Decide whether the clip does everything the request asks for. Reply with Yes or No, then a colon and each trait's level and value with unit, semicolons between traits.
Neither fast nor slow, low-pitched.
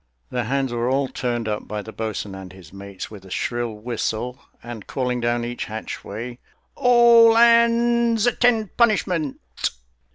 Yes: average, 150 wpm; low, 120 Hz